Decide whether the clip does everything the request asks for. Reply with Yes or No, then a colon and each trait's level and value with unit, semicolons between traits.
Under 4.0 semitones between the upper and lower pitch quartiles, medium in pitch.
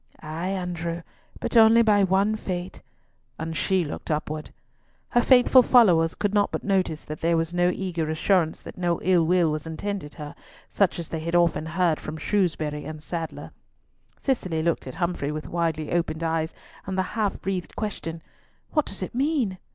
Yes: average, 3.4 semitones; medium, 175 Hz